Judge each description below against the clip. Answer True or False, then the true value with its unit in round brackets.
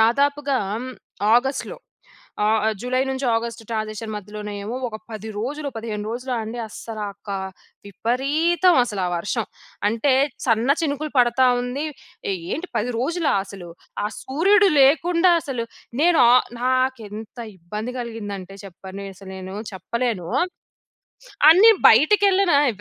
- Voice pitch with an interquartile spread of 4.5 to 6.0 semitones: True (5.0 semitones)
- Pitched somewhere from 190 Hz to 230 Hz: False (240 Hz)